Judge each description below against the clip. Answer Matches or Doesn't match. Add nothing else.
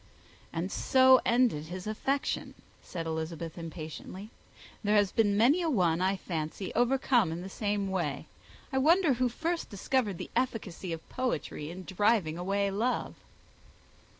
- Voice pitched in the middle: Doesn't match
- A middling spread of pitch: Doesn't match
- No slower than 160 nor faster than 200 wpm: Doesn't match